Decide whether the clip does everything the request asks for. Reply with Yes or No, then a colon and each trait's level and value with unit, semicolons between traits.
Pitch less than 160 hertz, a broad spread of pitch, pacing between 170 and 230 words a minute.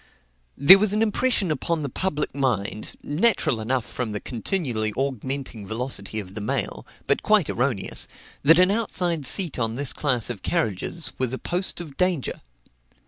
No: medium, 140 Hz; wide, 7.4 semitones; average, 160 wpm